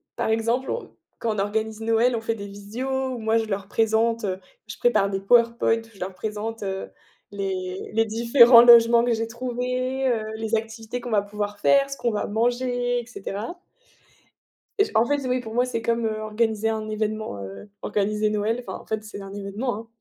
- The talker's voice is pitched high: Yes, high, 225 Hz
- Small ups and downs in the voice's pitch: Yes, narrow, 2.2 semitones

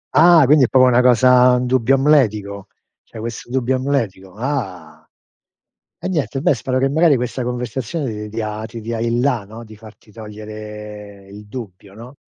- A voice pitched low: Yes, low, 120 Hz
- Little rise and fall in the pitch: No, average, 3.6 semitones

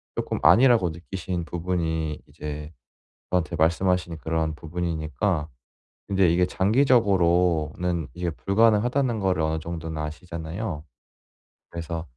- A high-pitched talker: No, very low, 85 Hz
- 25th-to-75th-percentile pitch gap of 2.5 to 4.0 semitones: Yes, average, 2.9 semitones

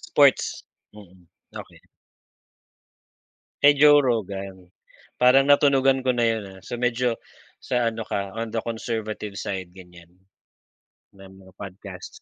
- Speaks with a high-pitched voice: No, low, 110 Hz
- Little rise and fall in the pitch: No, average, 4.5 semitones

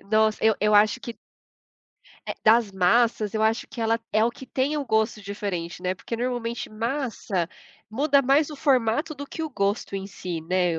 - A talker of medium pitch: No, high, 220 Hz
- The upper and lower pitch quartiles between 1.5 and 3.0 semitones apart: No, average, 4.1 semitones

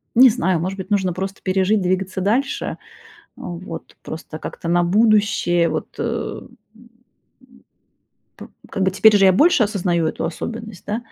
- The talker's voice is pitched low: No, high, 190 Hz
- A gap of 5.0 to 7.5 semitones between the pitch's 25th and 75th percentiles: No, average, 3.7 semitones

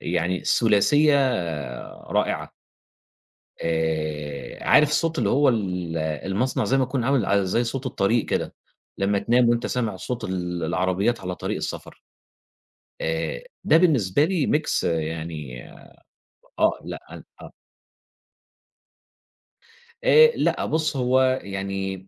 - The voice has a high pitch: No, low, 100 Hz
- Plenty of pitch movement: Yes, wide, 7.1 semitones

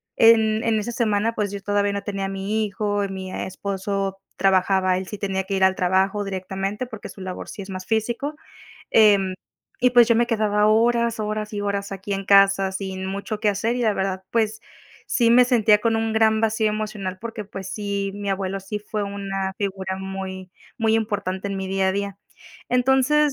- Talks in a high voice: Yes, high, 200 Hz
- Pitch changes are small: Yes, narrow, 2.3 semitones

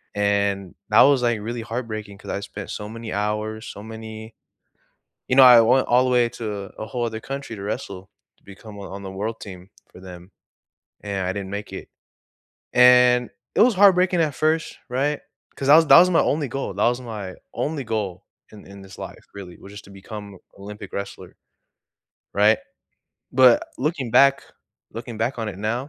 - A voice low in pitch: Yes, low, 110 Hz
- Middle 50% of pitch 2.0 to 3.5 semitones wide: No, average, 3.9 semitones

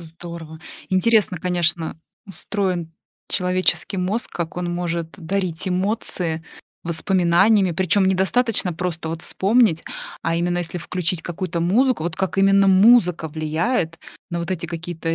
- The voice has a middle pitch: Yes, medium, 180 Hz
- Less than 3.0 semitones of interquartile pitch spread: Yes, narrow, 2.5 semitones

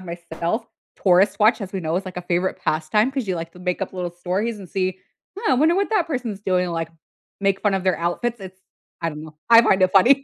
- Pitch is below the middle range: No, high, 190 Hz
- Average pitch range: Yes, average, 4.1 semitones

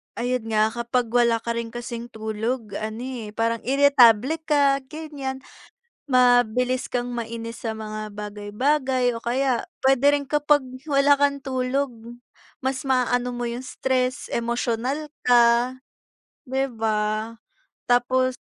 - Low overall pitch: No, high, 245 Hz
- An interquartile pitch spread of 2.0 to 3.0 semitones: Yes, narrow, 2.5 semitones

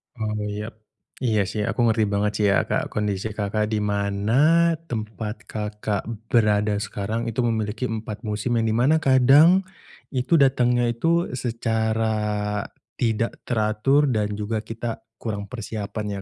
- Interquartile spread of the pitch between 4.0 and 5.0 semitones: No, narrow, 2.4 semitones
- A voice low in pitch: Yes, low, 110 Hz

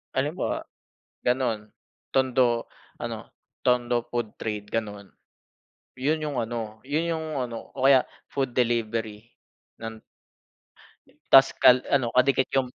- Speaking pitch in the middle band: No, low, 120 Hz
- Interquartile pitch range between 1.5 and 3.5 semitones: Yes, average, 2.8 semitones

